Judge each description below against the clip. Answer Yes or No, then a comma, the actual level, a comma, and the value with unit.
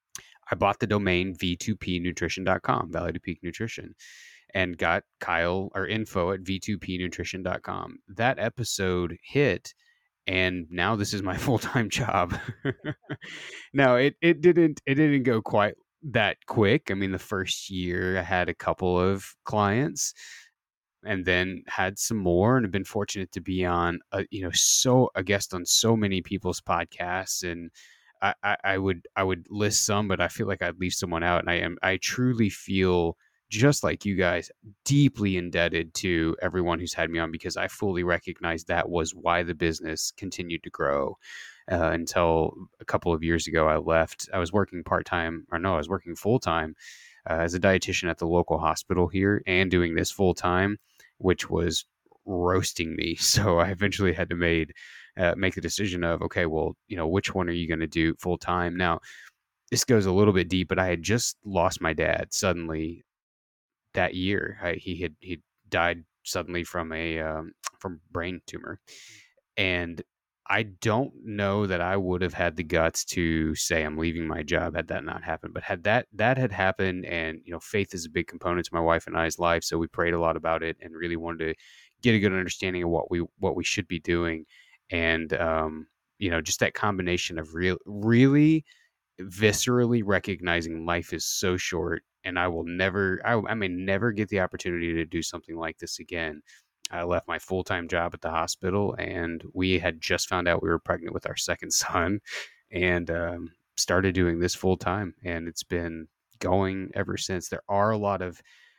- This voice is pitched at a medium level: No, very low, 90 Hz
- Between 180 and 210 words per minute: Yes, average, 190 wpm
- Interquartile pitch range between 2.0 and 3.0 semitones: Yes, narrow, 2.6 semitones